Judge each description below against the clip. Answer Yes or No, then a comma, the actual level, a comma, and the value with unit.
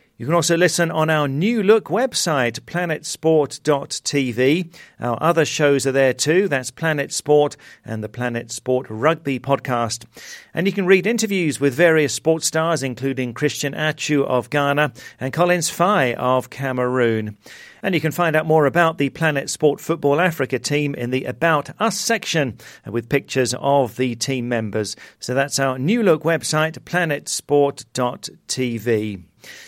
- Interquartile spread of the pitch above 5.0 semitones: No, average, 4.3 semitones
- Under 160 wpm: Yes, average, 150 wpm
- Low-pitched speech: No, medium, 145 Hz